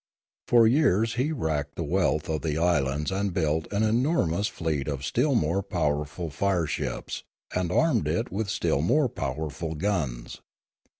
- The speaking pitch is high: No, very low, 85 Hz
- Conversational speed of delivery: Yes, average, 155 wpm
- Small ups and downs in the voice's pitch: No, wide, 5.4 semitones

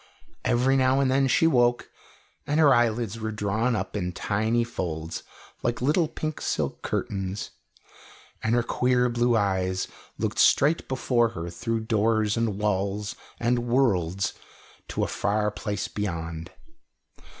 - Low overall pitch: Yes, low, 110 Hz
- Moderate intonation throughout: Yes, average, 3.7 semitones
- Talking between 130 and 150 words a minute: Yes, average, 140 wpm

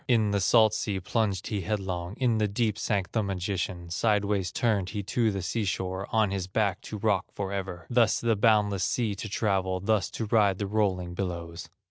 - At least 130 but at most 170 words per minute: No, average, 190 wpm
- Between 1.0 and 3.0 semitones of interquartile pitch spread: Yes, narrow, 2.6 semitones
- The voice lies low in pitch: Yes, low, 100 Hz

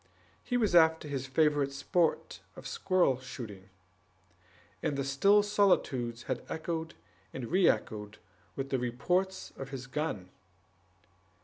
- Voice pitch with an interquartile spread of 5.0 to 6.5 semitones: Yes, wide, 5.6 semitones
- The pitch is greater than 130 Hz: Yes, medium, 140 Hz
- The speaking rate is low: Yes, slow, 125 wpm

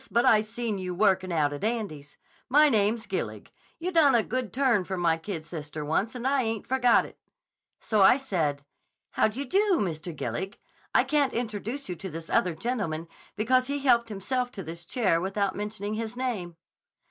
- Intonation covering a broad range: Yes, wide, 5.9 semitones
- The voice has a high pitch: Yes, high, 215 Hz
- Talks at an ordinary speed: Yes, average, 190 wpm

